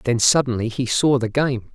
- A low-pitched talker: Yes, low, 125 Hz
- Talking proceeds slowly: No, fast, 205 wpm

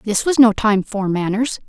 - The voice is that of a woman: Yes, female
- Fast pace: Yes, fast, 215 wpm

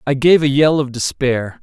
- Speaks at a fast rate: Yes, fast, 220 wpm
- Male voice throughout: Yes, male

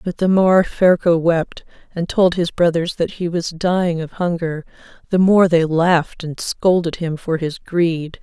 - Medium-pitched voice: Yes, medium, 170 Hz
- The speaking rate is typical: Yes, average, 180 wpm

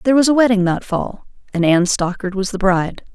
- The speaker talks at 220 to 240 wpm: Yes, fast, 230 wpm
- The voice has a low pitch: No, high, 200 Hz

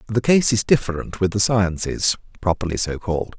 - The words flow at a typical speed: Yes, average, 175 wpm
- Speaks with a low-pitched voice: Yes, low, 100 Hz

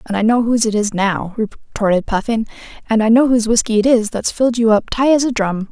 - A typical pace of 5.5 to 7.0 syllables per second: Yes, 6.0 syllables/s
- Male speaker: No, female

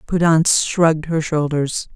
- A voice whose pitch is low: No, medium, 160 Hz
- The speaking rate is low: Yes, slow, 125 wpm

